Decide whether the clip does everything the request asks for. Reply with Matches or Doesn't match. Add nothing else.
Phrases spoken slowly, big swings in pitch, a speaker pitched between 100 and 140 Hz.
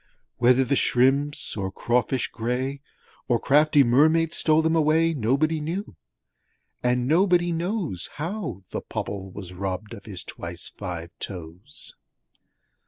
Matches